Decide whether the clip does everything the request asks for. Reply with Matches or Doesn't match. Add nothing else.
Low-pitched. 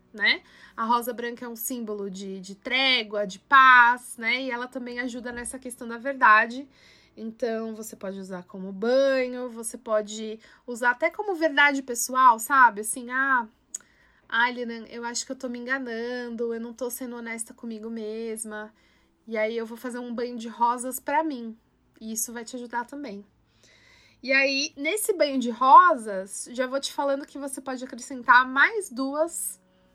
Doesn't match